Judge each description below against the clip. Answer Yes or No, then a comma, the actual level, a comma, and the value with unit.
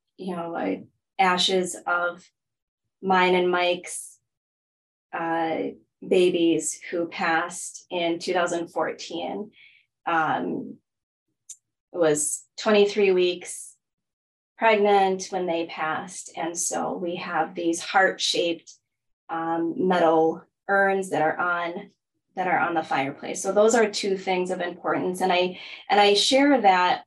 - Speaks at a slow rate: Yes, slow, 120 wpm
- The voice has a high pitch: No, medium, 175 Hz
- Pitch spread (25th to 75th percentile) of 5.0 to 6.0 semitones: No, narrow, 2.5 semitones